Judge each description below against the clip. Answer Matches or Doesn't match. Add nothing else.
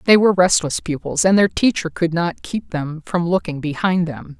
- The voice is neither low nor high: Matches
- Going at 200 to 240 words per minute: Matches